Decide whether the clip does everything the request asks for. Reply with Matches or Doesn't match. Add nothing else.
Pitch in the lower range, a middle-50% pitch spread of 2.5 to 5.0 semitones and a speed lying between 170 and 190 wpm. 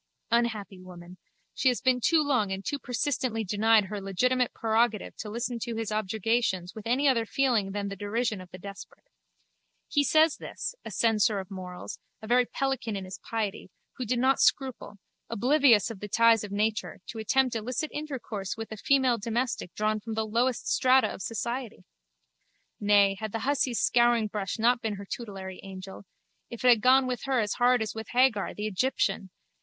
Doesn't match